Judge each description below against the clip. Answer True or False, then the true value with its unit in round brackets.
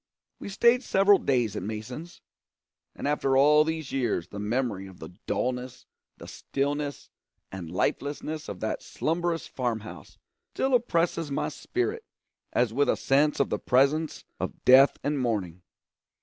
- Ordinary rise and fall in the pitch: False (6.0 semitones)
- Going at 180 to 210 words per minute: False (150 wpm)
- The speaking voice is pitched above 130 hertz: True (140 Hz)